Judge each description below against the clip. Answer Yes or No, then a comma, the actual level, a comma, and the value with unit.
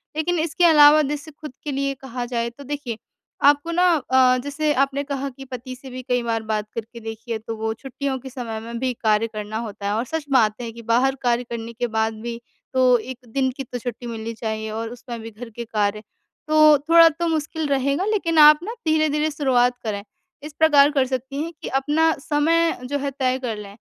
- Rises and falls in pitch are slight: No, average, 4.2 semitones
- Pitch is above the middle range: Yes, very high, 260 Hz